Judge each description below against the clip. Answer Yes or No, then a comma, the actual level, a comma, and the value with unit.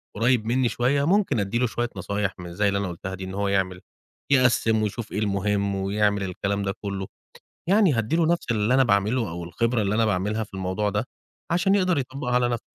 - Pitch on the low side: Yes, low, 105 Hz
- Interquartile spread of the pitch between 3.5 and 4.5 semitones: Yes, average, 3.9 semitones